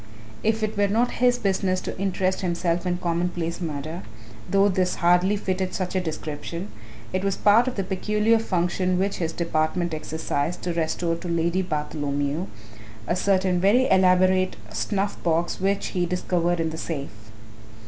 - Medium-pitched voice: Yes, medium, 180 Hz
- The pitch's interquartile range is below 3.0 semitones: Yes, narrow, 2.5 semitones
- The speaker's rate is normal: Yes, average, 160 wpm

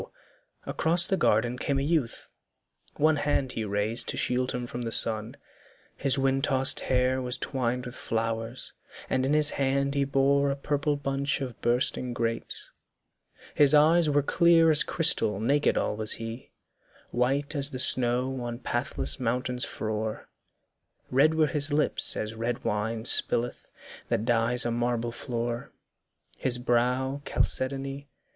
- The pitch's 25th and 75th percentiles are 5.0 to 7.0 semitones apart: No, average, 3.0 semitones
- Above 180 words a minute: No, average, 150 wpm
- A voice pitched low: Yes, low, 130 Hz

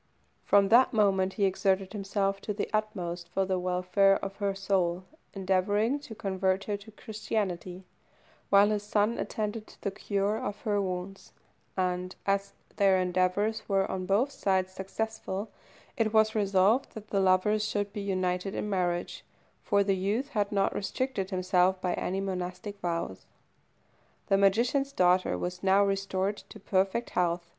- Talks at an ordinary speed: Yes, average, 155 wpm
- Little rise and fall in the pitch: Yes, narrow, 1.9 semitones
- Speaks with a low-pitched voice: No, high, 195 Hz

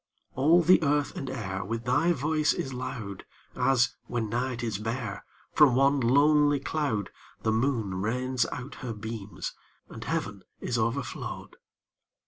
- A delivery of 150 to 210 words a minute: No, average, 140 wpm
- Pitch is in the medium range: No, low, 125 Hz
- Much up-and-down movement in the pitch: No, average, 4.0 semitones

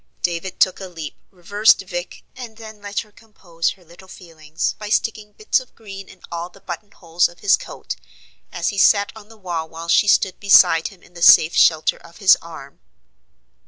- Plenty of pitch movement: No, average, 3.5 semitones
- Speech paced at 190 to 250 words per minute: Yes, average, 195 wpm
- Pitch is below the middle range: No, medium, 185 Hz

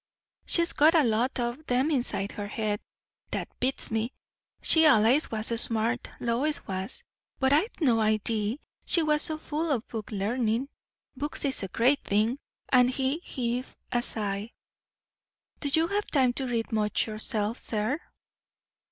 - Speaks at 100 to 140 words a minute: No, average, 150 wpm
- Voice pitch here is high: Yes, high, 245 Hz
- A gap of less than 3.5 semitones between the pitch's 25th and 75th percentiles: No, average, 4.7 semitones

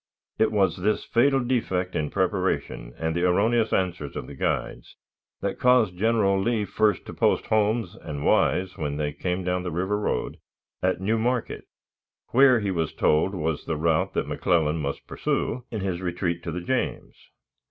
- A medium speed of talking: Yes, average, 175 wpm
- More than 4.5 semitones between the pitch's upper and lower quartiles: Yes, average, 4.9 semitones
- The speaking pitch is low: Yes, very low, 95 Hz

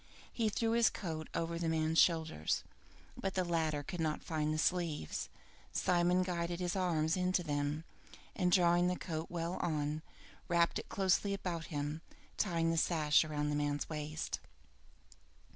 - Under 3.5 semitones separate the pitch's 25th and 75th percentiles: Yes, narrow, 2.6 semitones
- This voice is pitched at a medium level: Yes, medium, 165 Hz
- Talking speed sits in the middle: Yes, average, 155 wpm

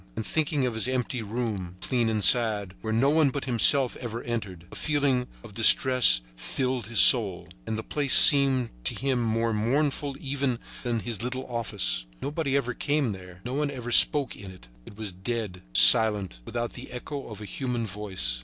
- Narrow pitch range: No, average, 4.0 semitones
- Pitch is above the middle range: No, low, 120 Hz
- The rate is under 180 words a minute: No, average, 185 wpm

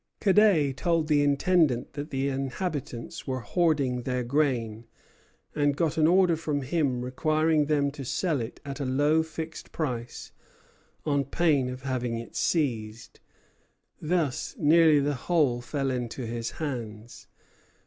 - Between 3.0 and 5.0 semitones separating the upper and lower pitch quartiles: Yes, average, 4.0 semitones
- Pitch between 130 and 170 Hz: Yes, medium, 140 Hz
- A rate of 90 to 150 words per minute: Yes, average, 140 wpm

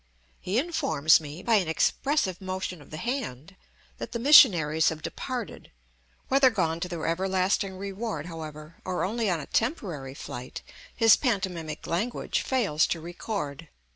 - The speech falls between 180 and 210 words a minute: No, average, 145 wpm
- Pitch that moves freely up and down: Yes, wide, 6.1 semitones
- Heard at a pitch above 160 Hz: Yes, medium, 185 Hz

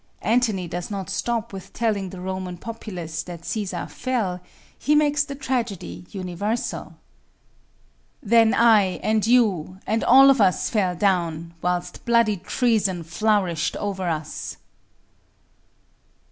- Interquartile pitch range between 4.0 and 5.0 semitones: Yes, average, 4.4 semitones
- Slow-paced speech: Yes, slow, 120 wpm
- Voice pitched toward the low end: No, high, 200 Hz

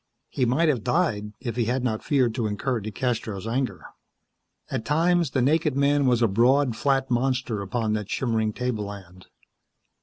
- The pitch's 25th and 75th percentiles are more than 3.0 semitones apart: Yes, average, 3.7 semitones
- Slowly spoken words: No, average, 160 wpm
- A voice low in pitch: Yes, low, 125 Hz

